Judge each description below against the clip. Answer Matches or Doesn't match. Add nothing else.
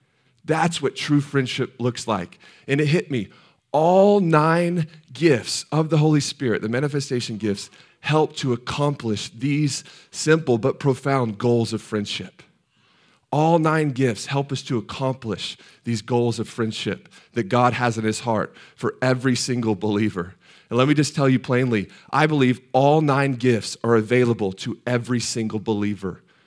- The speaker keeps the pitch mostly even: Doesn't match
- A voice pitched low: Matches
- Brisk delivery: Doesn't match